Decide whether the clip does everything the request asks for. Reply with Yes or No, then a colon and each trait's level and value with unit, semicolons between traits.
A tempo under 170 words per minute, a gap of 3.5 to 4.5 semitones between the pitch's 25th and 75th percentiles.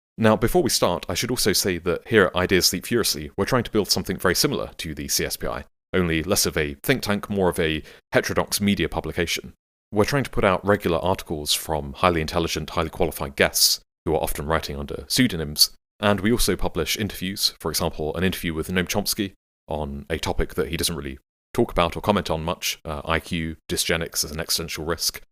No: fast, 205 wpm; average, 4.2 semitones